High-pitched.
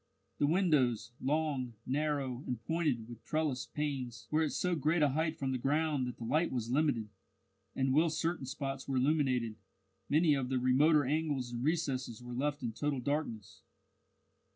No: low, 135 Hz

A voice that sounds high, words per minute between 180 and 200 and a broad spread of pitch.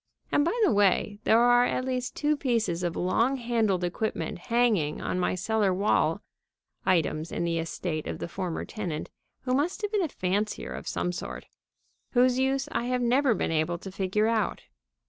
Yes: high, 215 Hz; average, 185 wpm; wide, 5.7 semitones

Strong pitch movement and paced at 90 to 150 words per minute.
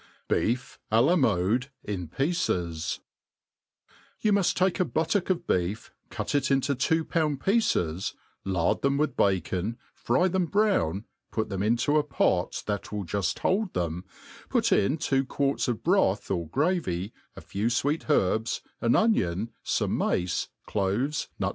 Yes: wide, 9.0 semitones; average, 145 wpm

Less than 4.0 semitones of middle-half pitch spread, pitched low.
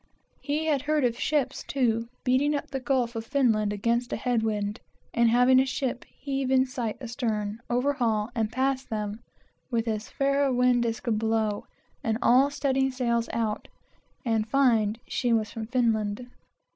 No: average, 3.1 semitones; high, 240 Hz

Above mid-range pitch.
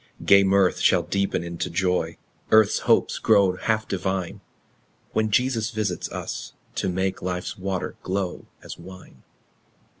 No: very low, 95 Hz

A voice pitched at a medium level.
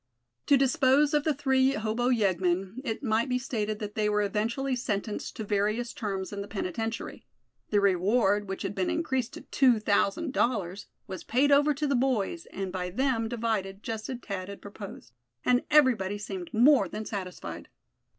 No: high, 220 Hz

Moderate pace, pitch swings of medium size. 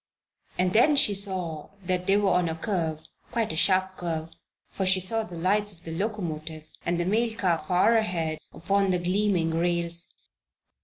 Yes: average, 175 wpm; average, 3.3 semitones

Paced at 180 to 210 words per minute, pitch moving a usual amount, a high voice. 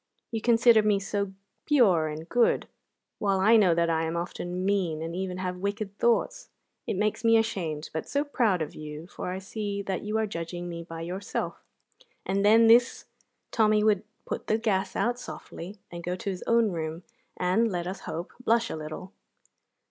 Yes: average, 185 wpm; average, 4.2 semitones; high, 195 Hz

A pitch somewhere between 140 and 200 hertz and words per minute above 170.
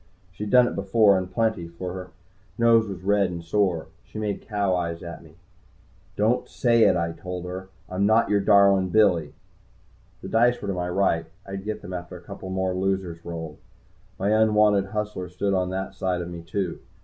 No: very low, 95 Hz; average, 195 wpm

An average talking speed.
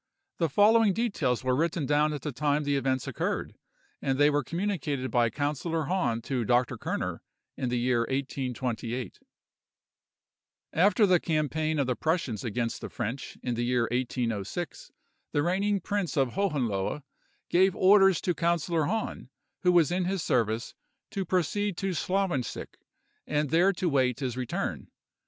Yes: average, 150 wpm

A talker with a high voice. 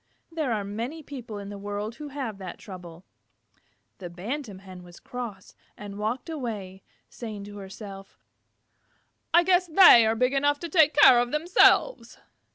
Yes: high, 225 Hz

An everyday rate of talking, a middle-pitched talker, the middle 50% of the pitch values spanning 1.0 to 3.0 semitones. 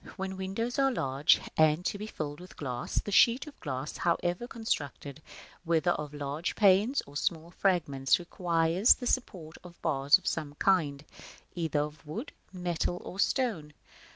No: average, 155 wpm; medium, 170 Hz; average, 4.6 semitones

